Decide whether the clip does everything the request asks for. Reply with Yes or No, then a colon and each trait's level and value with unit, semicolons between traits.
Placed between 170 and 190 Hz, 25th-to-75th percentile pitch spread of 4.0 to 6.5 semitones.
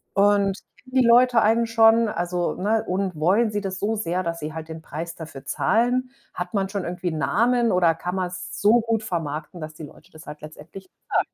Yes: medium, 185 Hz; average, 5.1 semitones